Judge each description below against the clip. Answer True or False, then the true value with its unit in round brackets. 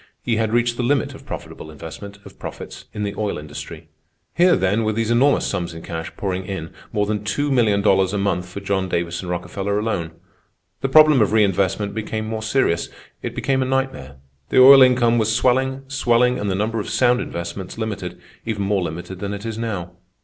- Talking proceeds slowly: False (190 wpm)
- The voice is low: True (105 Hz)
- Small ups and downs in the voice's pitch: False (4.2 semitones)